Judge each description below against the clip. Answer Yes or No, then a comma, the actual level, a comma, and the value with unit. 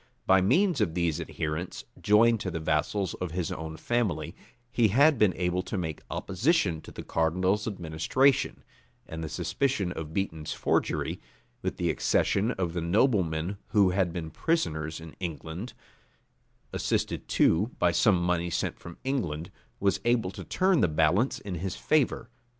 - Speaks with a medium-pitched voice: No, very low, 90 Hz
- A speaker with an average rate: Yes, average, 155 wpm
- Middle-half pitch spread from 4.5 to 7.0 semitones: Yes, average, 4.9 semitones